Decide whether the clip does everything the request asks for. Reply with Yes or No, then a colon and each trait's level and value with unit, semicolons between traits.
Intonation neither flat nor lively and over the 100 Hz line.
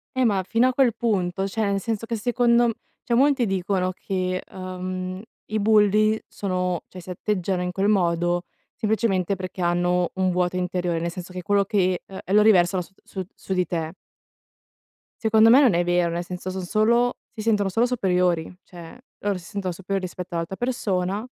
Yes: average, 3.0 semitones; high, 190 Hz